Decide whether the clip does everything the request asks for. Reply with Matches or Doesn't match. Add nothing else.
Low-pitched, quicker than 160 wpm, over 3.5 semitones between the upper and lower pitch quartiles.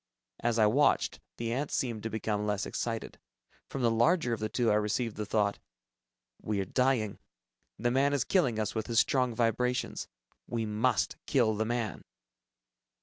Doesn't match